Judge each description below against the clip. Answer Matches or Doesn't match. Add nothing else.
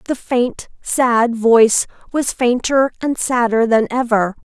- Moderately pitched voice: Doesn't match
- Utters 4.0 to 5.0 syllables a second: Doesn't match